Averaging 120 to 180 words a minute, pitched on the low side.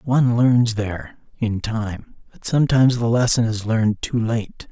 Yes: average, 140 wpm; low, 115 Hz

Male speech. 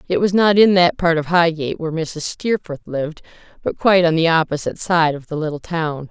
No: female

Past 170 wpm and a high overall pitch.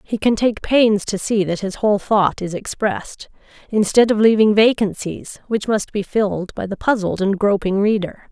Yes: average, 190 wpm; high, 205 Hz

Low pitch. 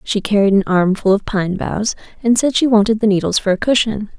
No: high, 210 Hz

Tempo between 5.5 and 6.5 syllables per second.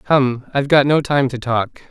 No: 4.8 syllables/s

